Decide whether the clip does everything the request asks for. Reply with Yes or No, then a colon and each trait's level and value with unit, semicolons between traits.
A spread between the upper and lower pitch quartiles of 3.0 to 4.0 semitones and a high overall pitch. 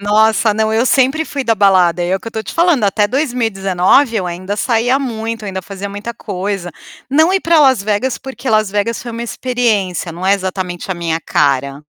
No: average, 4.5 semitones; high, 215 Hz